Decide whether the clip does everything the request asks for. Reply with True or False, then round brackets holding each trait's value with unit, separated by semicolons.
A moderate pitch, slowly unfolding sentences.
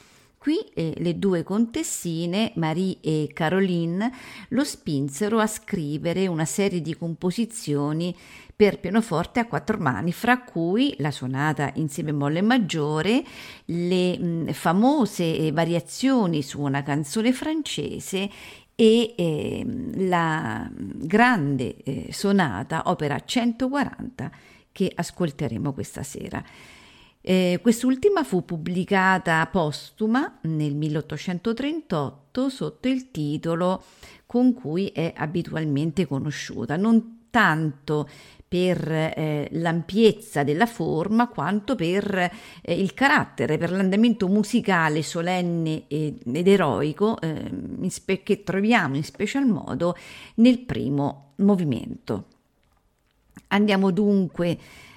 True (180 Hz; 105 wpm)